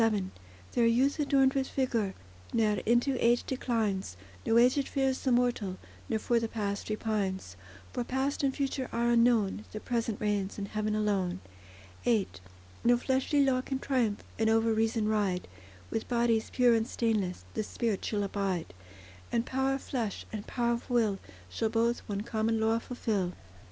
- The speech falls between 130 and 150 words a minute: No, average, 165 wpm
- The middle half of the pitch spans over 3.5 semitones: No, average, 2.8 semitones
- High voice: Yes, high, 225 Hz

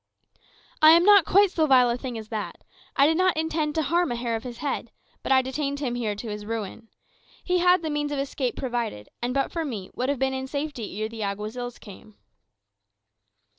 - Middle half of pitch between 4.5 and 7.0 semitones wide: Yes, average, 5.2 semitones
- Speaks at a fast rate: Yes, fast, 215 wpm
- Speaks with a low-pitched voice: No, very high, 260 Hz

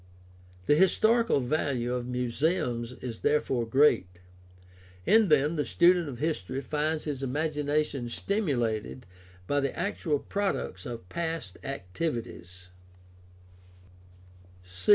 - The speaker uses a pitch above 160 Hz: No, medium, 140 Hz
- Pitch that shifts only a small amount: No, average, 4.9 semitones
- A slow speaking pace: Yes, slow, 105 wpm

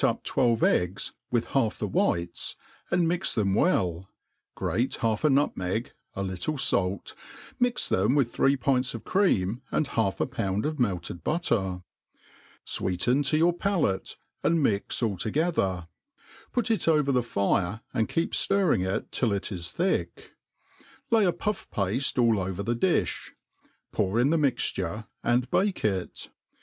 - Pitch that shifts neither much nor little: No, wide, 8.0 semitones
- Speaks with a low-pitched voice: Yes, low, 115 Hz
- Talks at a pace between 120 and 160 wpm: Yes, average, 155 wpm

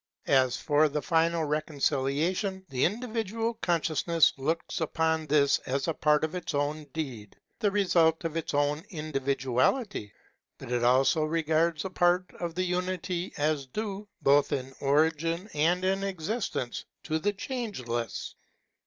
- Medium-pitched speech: Yes, medium, 160 Hz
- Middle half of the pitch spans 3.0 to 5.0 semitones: Yes, average, 4.2 semitones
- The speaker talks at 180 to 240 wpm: No, average, 145 wpm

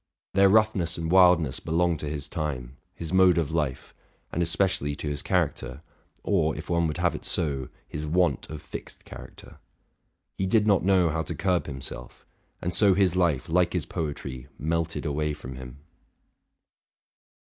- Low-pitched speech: Yes, very low, 80 Hz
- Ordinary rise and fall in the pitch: Yes, average, 3.6 semitones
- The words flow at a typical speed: Yes, average, 165 wpm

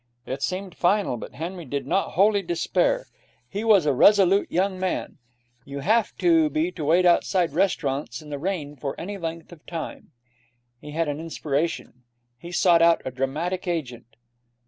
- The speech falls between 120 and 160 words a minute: No, average, 170 wpm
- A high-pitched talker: No, medium, 170 Hz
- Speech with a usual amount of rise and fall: Yes, average, 4.7 semitones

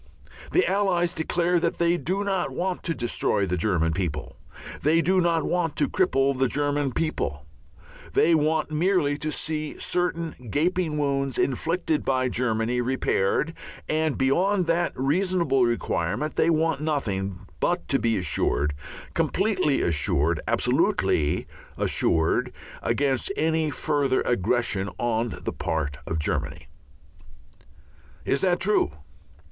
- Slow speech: Yes, slow, 125 wpm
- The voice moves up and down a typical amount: No, wide, 6.5 semitones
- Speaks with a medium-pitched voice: Yes, medium, 145 Hz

